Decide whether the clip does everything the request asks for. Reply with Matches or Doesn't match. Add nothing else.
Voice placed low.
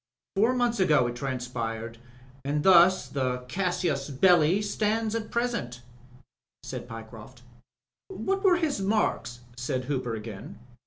Doesn't match